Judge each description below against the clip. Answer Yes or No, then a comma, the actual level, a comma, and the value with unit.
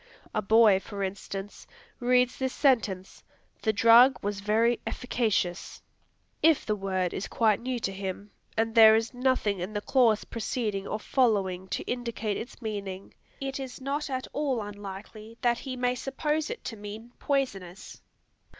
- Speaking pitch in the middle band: No, high, 220 Hz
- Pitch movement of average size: Yes, average, 3.9 semitones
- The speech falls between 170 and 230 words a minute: No, average, 155 wpm